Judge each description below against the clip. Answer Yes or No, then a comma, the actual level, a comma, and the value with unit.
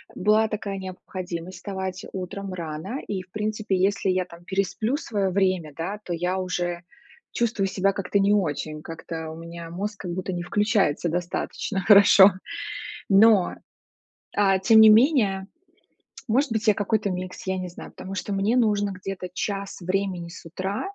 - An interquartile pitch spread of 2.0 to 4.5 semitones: Yes, narrow, 2.4 semitones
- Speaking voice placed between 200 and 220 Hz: No, high, 190 Hz